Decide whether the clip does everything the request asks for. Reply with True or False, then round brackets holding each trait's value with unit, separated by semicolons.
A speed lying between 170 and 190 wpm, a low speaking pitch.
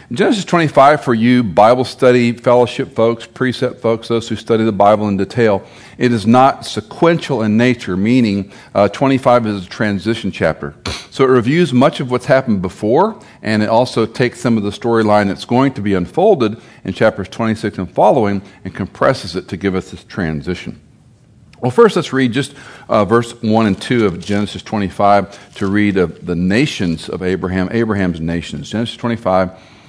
True (175 wpm; 110 Hz)